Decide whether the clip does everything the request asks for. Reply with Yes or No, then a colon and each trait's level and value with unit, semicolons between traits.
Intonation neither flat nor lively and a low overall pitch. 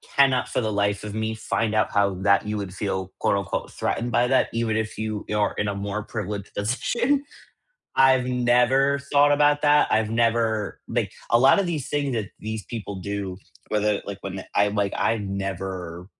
Yes: average, 3.6 semitones; low, 110 Hz